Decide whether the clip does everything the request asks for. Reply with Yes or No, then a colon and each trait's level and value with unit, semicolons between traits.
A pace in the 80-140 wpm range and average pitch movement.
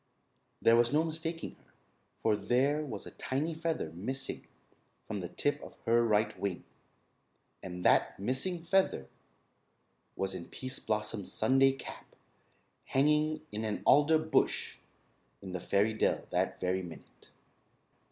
No: slow, 135 wpm; wide, 6.8 semitones